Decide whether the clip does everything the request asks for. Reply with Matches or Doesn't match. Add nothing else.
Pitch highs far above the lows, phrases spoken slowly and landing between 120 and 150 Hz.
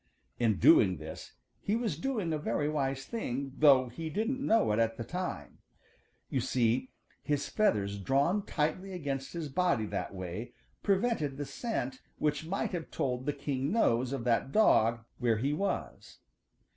Doesn't match